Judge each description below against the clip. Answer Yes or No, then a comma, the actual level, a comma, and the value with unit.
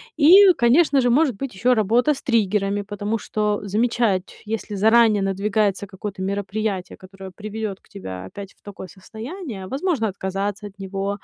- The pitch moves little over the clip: No, average, 3.2 semitones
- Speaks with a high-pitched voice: Yes, high, 210 Hz